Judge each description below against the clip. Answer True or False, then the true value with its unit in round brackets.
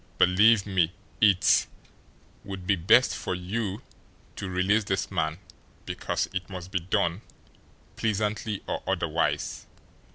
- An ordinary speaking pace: False (120 wpm)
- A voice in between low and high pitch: False (95 Hz)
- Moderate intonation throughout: False (2.3 semitones)